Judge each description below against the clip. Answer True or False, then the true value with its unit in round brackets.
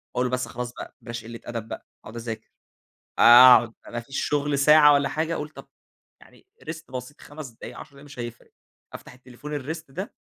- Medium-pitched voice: False (130 Hz)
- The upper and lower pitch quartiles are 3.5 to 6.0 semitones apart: True (3.8 semitones)